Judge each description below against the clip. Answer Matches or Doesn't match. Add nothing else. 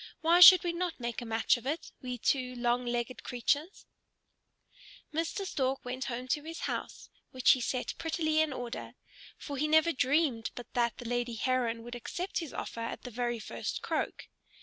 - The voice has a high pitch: Matches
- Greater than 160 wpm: Matches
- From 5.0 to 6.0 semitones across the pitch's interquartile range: Doesn't match